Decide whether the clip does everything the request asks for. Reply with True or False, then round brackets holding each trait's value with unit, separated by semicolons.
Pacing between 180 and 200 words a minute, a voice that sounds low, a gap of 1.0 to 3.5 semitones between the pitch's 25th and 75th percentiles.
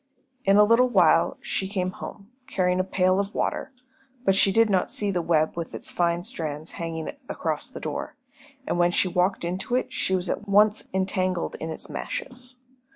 False (190 wpm; 185 Hz; 2.9 semitones)